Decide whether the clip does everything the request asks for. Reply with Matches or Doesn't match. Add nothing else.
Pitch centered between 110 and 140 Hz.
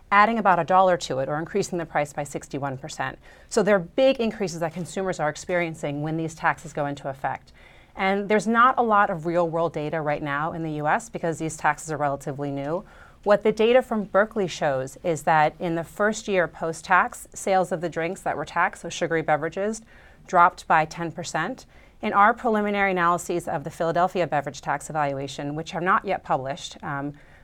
Doesn't match